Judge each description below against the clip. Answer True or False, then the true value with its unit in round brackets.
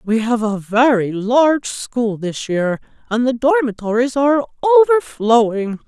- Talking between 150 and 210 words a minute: False (135 wpm)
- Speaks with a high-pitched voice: True (240 Hz)